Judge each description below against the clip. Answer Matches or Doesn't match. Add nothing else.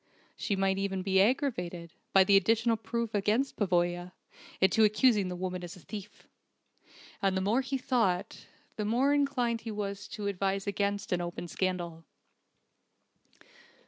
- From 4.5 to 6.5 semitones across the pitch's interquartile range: Doesn't match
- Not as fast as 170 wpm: Matches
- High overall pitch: Matches